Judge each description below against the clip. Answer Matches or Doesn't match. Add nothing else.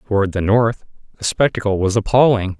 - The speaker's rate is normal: Matches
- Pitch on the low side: Matches